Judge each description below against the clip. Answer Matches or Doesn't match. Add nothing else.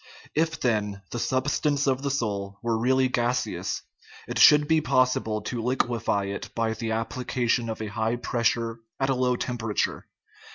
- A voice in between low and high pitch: Doesn't match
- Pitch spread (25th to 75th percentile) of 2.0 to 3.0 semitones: Matches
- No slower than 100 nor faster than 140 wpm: Doesn't match